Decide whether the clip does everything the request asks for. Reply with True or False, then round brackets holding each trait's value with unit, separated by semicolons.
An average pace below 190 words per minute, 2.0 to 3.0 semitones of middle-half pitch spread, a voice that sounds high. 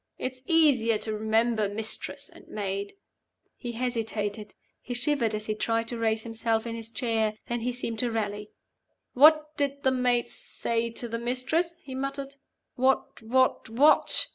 True (165 wpm; 2.7 semitones; 235 Hz)